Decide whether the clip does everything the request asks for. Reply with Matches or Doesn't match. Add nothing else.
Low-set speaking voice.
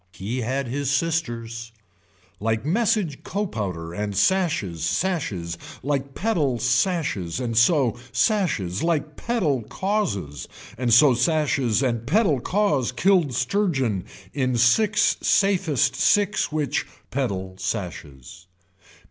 Matches